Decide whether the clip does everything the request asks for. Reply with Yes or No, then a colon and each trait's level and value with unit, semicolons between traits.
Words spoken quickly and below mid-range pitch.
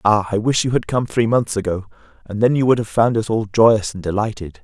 Yes: fast, 245 wpm; low, 110 Hz